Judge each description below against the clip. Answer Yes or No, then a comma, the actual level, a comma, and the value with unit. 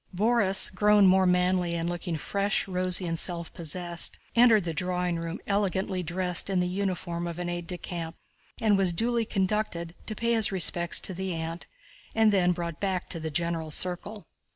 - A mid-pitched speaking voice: Yes, medium, 180 Hz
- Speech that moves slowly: No, average, 180 wpm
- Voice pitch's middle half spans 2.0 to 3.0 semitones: Yes, narrow, 2.5 semitones